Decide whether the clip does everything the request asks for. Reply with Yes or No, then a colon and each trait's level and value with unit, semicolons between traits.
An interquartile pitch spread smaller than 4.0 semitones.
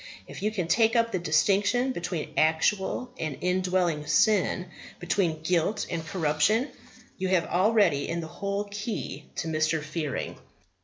No: average, 4.4 semitones